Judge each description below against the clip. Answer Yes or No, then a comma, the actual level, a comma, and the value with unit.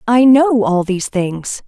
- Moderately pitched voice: No, high, 220 Hz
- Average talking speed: Yes, average, 180 wpm